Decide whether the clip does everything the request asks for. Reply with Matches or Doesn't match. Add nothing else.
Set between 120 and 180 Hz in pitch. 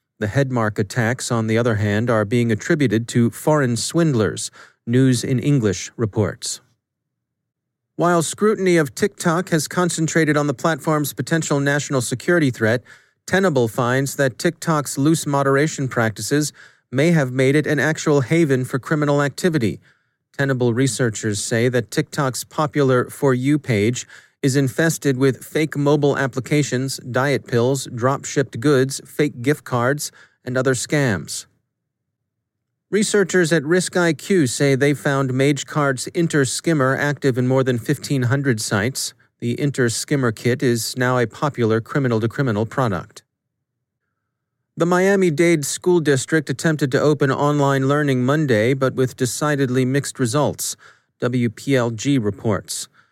Matches